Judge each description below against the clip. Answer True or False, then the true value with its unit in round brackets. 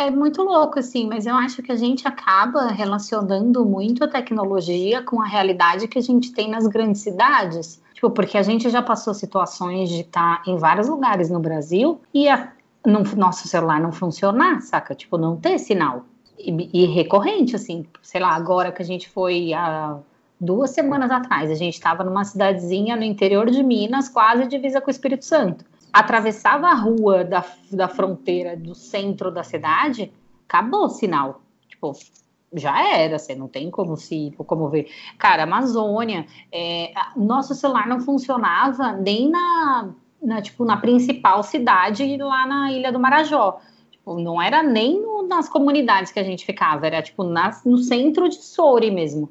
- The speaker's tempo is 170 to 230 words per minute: True (175 wpm)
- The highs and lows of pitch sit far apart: True (6.3 semitones)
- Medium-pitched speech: False (210 Hz)